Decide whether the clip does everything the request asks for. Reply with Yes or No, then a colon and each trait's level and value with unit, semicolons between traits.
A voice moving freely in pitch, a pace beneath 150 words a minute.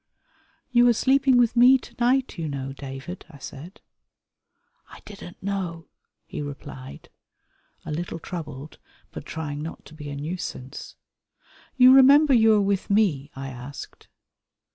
Yes: wide, 8.9 semitones; average, 140 wpm